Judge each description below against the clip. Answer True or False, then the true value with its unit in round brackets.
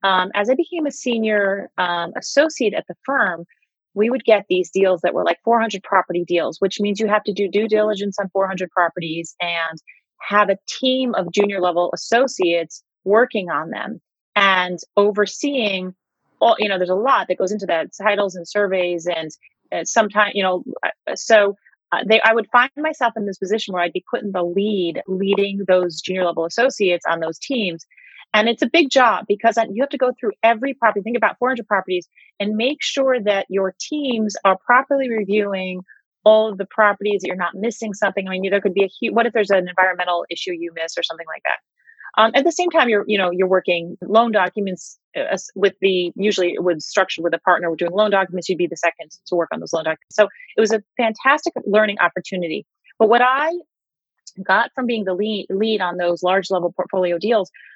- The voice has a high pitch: True (200 Hz)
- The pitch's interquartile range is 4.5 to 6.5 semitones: False (3.7 semitones)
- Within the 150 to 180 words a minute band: False (205 wpm)